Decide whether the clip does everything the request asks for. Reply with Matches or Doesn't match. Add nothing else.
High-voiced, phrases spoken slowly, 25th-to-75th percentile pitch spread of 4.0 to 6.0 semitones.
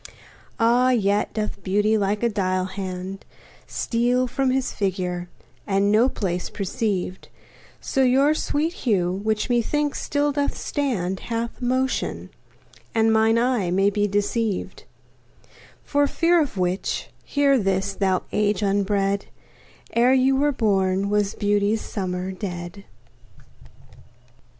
Matches